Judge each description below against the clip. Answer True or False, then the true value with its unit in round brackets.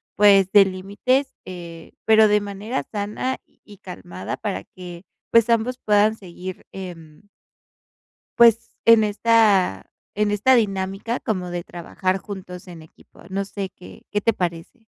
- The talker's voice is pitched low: False (200 Hz)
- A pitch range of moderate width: True (3.2 semitones)